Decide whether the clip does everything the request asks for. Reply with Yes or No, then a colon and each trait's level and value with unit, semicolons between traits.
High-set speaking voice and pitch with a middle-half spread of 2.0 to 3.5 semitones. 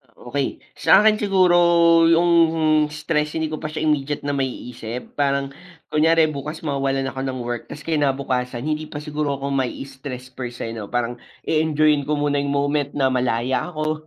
No: medium, 145 Hz; average, 2.7 semitones